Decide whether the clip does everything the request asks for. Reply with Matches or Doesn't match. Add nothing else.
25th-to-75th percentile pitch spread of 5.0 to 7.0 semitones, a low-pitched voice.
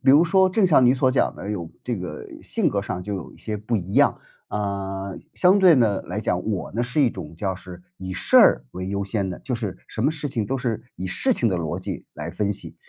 Matches